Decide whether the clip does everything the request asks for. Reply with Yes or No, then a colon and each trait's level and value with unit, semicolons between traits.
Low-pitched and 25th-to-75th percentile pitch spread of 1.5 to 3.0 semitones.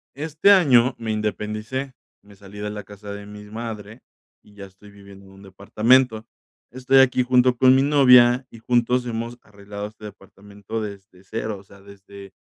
No: low, 105 Hz; average, 3.6 semitones